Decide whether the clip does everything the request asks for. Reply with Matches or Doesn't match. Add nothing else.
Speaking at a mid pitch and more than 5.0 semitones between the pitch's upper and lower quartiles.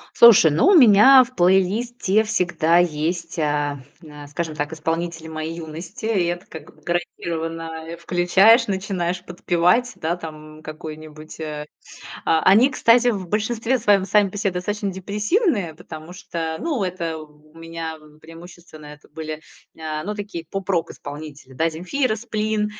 Doesn't match